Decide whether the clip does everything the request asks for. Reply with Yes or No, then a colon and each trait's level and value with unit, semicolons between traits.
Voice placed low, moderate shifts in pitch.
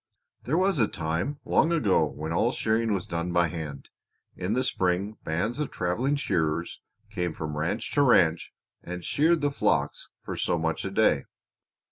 No: very low, 90 Hz; wide, 7.1 semitones